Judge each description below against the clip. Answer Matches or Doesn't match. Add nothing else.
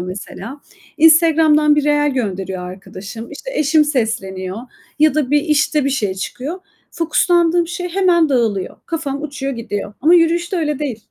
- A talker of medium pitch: Doesn't match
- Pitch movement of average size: Doesn't match